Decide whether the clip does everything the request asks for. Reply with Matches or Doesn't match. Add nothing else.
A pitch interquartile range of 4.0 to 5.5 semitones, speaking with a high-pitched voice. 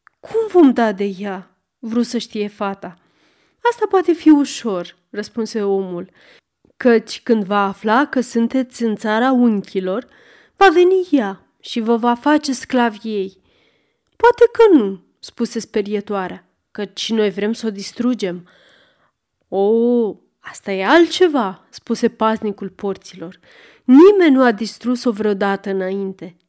Matches